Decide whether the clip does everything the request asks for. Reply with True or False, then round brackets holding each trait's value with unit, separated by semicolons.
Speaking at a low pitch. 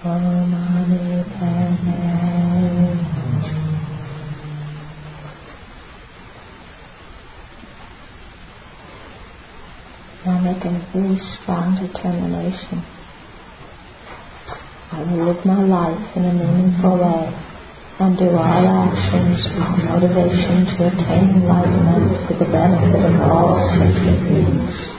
False (175 Hz)